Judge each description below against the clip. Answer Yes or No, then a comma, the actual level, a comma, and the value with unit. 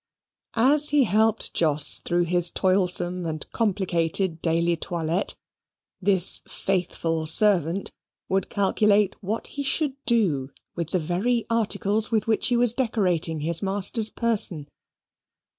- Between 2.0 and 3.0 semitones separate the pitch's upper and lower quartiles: No, average, 4.5 semitones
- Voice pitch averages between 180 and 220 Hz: Yes, high, 190 Hz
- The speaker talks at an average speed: No, slow, 125 wpm